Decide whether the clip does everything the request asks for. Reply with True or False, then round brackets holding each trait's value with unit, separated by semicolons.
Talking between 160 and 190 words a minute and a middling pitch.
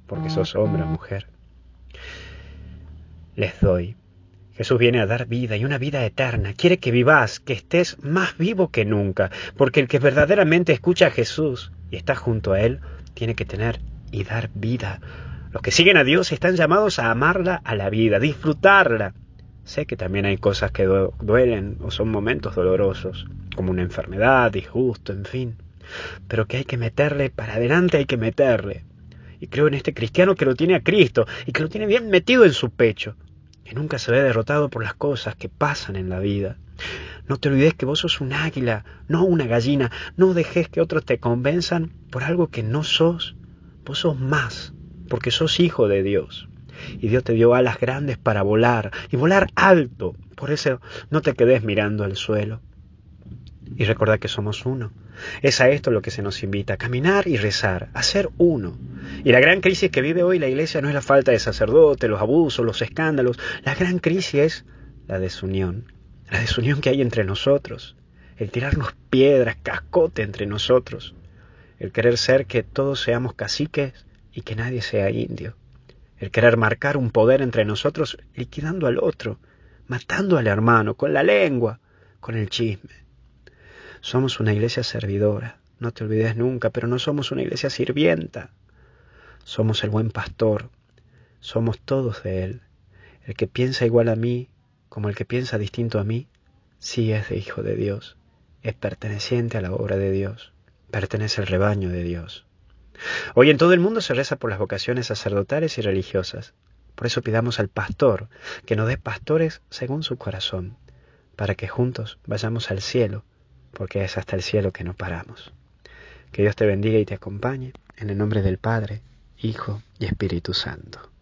False (180 wpm; 115 Hz)